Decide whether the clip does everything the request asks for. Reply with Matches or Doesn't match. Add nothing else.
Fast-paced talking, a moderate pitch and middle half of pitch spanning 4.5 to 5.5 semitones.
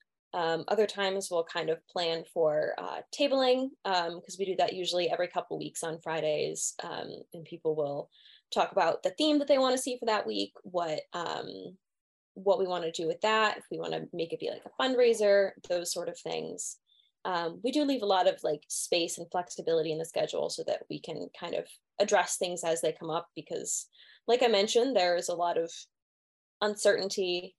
Matches